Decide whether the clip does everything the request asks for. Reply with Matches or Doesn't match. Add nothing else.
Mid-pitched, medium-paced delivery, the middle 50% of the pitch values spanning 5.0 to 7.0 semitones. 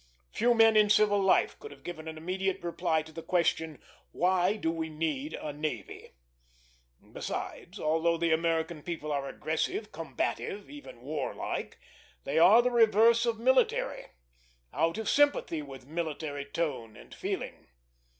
Matches